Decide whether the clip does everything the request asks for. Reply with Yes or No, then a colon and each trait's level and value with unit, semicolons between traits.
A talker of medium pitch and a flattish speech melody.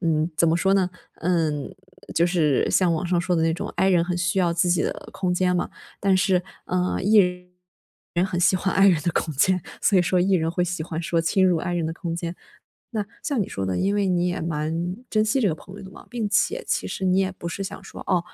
Yes: medium, 180 Hz; narrow, 2.2 semitones